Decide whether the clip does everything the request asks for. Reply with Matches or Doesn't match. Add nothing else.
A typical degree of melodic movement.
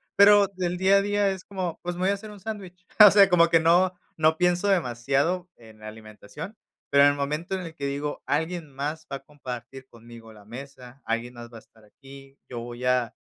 Doesn't match